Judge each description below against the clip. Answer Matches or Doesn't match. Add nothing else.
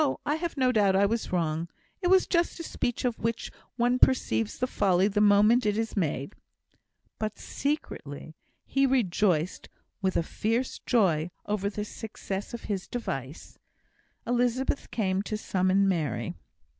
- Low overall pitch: Doesn't match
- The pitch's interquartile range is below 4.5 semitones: Doesn't match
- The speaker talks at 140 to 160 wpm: Matches